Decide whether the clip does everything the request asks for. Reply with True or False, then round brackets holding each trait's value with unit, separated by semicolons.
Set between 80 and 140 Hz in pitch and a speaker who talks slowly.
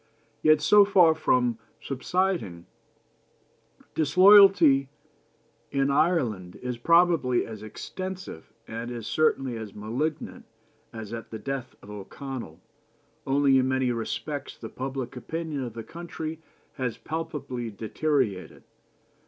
True (135 Hz; 110 wpm)